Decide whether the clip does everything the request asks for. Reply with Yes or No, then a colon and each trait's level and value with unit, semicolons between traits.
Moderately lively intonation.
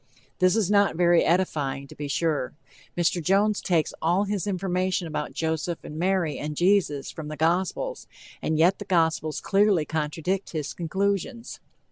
Yes: average, 3.6 semitones